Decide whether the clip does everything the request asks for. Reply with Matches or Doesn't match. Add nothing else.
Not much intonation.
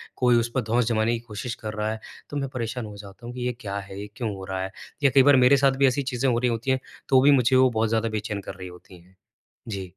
Doesn't match